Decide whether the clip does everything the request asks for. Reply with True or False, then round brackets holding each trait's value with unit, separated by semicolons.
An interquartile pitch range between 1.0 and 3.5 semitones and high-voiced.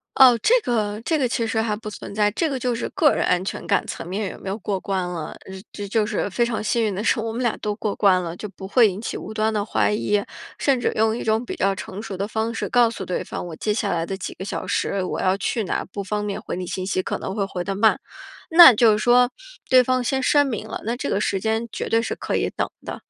True (3.1 semitones; 215 Hz)